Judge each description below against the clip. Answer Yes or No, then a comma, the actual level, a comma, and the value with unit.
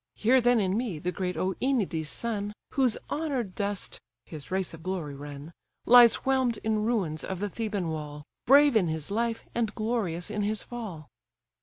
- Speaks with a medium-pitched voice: No, high, 205 Hz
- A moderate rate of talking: Yes, average, 170 wpm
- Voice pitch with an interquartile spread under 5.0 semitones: No, wide, 5.6 semitones